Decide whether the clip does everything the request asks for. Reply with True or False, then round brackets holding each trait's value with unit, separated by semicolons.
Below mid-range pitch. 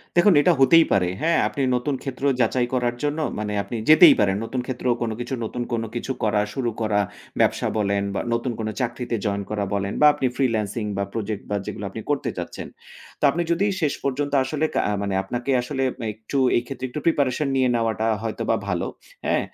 True (120 Hz)